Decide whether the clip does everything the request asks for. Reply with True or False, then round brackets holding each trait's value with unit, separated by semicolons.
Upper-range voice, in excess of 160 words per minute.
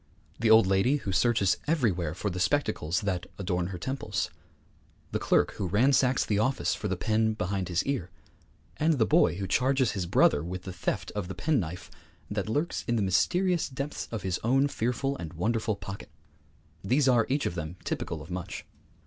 False (105 Hz; 190 wpm)